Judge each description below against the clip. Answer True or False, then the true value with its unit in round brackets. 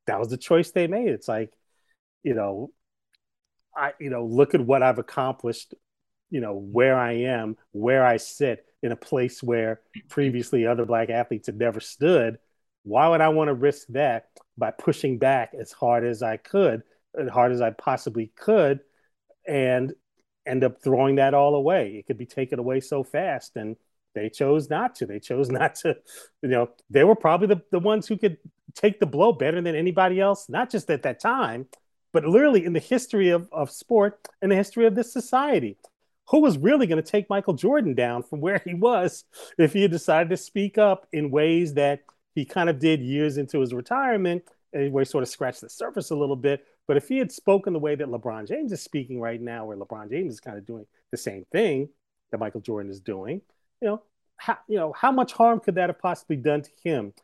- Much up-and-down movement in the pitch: True (7.7 semitones)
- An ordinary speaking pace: False (210 wpm)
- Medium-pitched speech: True (150 Hz)